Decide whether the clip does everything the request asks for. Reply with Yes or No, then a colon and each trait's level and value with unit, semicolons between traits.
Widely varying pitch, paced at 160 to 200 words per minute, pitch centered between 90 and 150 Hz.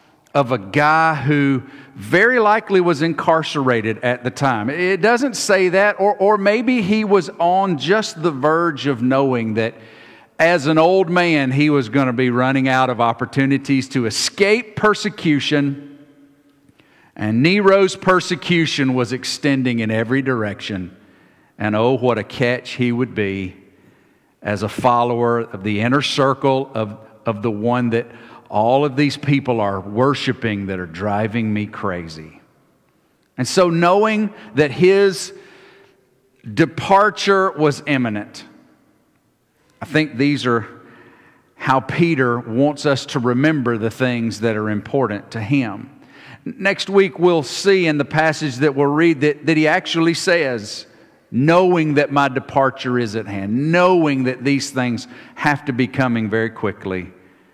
No: wide, 5.7 semitones; average, 145 wpm; medium, 140 Hz